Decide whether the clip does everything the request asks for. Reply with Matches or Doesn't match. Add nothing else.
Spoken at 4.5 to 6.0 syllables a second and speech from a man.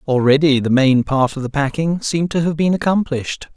Matches